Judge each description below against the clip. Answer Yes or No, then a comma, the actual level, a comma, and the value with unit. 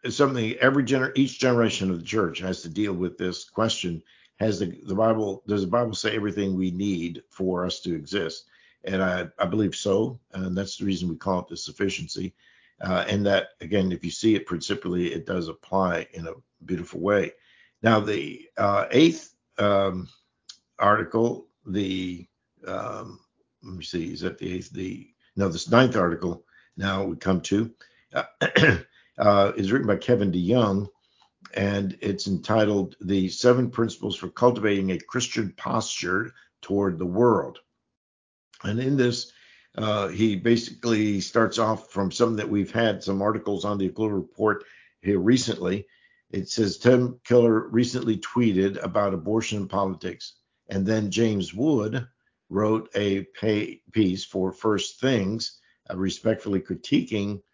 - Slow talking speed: No, average, 155 wpm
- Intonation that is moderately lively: Yes, average, 3.1 semitones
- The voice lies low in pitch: Yes, low, 100 Hz